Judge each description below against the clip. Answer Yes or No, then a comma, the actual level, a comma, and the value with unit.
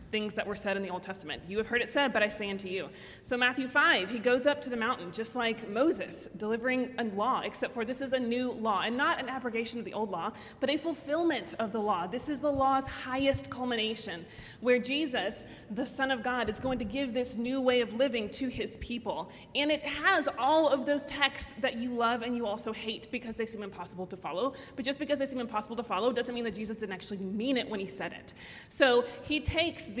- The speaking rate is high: Yes, fast, 245 wpm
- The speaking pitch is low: No, high, 245 Hz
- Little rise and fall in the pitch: No, average, 3.7 semitones